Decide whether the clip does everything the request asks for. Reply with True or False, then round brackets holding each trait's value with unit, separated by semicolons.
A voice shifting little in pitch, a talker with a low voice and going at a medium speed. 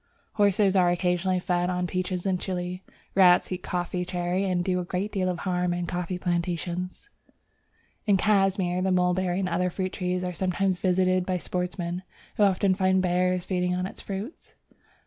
False (1.0 semitones; 180 Hz; 175 wpm)